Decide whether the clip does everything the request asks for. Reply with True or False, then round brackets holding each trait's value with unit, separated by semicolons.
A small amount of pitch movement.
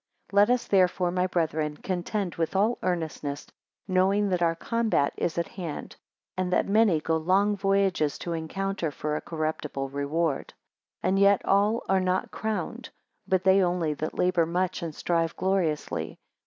False (3.3 semitones)